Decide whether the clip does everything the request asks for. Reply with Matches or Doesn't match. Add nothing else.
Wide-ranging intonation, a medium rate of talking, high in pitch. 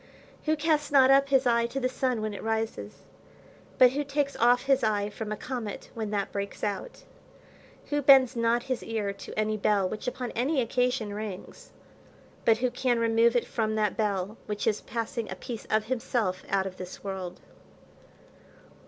Doesn't match